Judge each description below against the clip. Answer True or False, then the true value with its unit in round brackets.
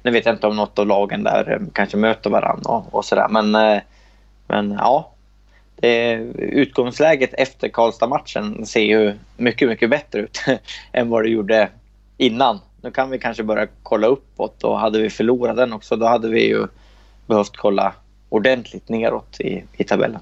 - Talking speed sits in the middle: True (165 wpm)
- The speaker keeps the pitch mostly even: True (2.0 semitones)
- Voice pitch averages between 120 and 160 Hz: False (110 Hz)